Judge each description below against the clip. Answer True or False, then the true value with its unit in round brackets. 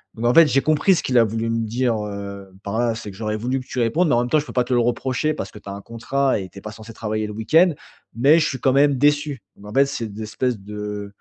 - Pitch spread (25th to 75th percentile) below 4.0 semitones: False (4.3 semitones)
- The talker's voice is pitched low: True (115 Hz)